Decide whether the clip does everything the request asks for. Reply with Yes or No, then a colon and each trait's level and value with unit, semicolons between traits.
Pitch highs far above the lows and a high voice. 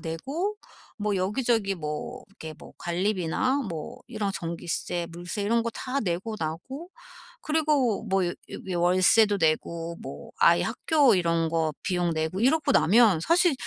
Yes: wide, 6.5 semitones; high, 195 Hz